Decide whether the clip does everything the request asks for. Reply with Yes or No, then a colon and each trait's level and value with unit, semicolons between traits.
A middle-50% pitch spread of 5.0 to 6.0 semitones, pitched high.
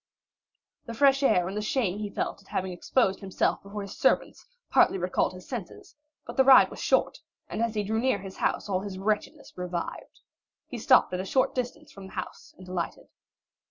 No: average, 4.5 semitones; high, 200 Hz